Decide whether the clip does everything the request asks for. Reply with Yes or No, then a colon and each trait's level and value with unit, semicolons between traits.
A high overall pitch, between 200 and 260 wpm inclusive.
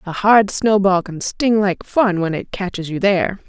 Yes: high, 195 Hz; fast, 205 wpm